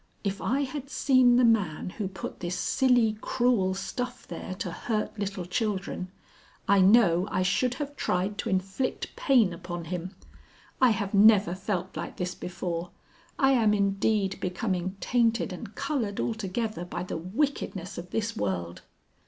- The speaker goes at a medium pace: Yes, average, 155 wpm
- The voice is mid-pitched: No, high, 200 Hz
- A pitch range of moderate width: Yes, average, 4.2 semitones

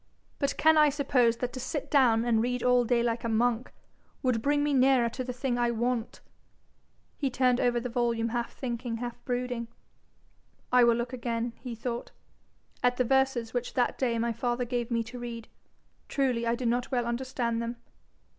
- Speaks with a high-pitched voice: Yes, high, 245 Hz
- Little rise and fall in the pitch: Yes, narrow, 1.5 semitones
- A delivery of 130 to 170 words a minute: No, average, 190 wpm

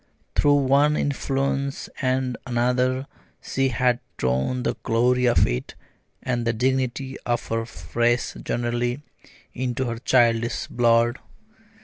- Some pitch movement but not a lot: No, narrow, 1.9 semitones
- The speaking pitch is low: Yes, low, 125 Hz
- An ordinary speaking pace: No, slow, 115 wpm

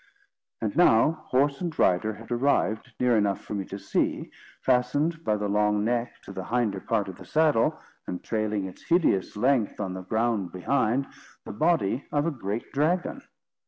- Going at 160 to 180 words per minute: Yes, average, 175 wpm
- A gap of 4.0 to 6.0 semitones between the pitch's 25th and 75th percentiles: Yes, wide, 5.4 semitones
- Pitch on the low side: Yes, low, 115 Hz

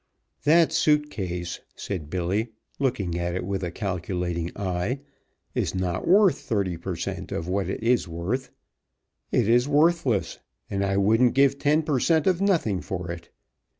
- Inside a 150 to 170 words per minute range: Yes, average, 160 wpm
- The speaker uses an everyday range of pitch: No, wide, 7.7 semitones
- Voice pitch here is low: Yes, low, 100 Hz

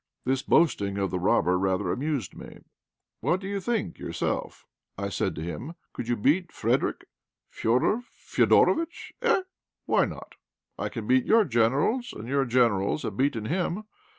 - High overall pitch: No, low, 135 Hz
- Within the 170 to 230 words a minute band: No, average, 155 wpm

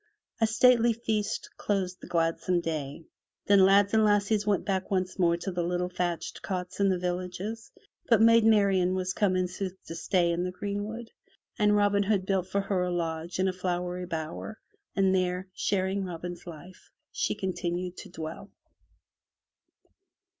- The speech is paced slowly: No, average, 165 wpm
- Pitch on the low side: No, medium, 185 Hz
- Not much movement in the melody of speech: Yes, narrow, 2.3 semitones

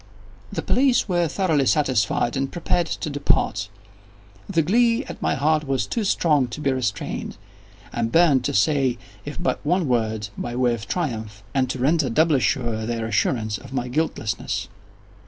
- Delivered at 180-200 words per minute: No, average, 165 wpm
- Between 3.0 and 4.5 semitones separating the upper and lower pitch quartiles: No, wide, 5.5 semitones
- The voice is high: No, low, 135 Hz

